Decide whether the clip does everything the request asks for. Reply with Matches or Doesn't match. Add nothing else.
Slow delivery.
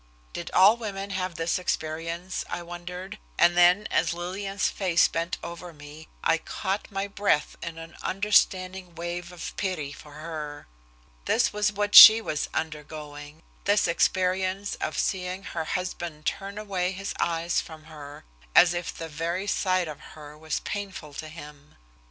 Doesn't match